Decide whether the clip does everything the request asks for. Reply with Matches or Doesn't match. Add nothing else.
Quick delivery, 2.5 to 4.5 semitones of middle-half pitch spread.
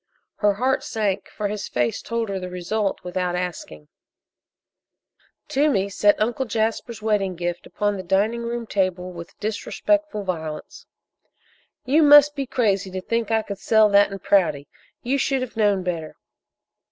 Doesn't match